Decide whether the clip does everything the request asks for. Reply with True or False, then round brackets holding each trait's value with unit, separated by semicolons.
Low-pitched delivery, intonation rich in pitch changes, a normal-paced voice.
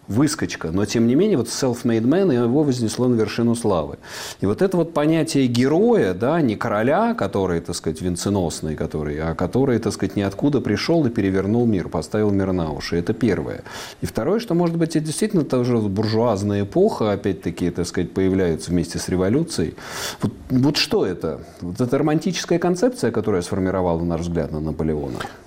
False (105 Hz; 6.7 semitones; 175 wpm)